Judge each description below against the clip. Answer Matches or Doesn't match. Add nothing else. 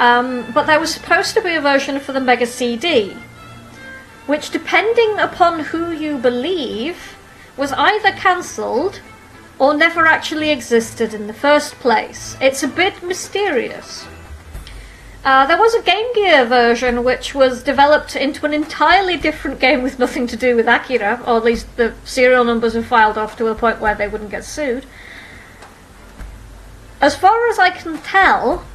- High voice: Matches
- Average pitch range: Doesn't match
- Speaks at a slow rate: Doesn't match